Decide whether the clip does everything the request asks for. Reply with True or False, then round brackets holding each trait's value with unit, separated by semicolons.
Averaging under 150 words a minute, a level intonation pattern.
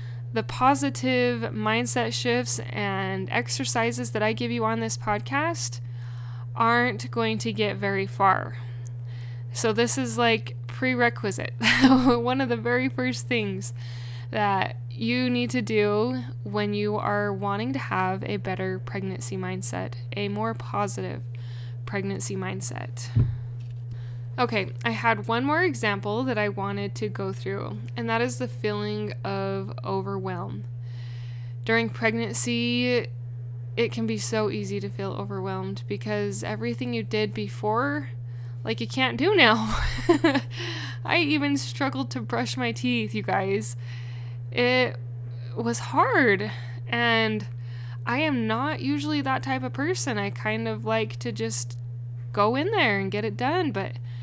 True (135 wpm; 1.7 semitones)